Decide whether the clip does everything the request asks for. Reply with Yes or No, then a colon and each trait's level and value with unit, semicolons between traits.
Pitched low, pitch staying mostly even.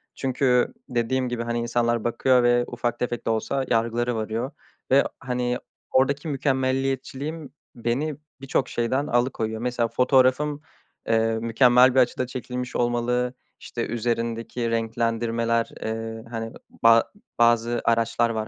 Yes: low, 120 Hz; narrow, 1.9 semitones